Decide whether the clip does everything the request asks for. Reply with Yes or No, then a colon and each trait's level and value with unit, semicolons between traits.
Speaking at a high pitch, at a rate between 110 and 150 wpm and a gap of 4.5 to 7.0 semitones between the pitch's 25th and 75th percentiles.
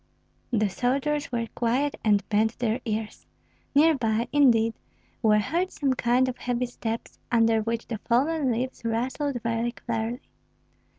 No: high, 235 Hz; average, 140 wpm; narrow, 2.6 semitones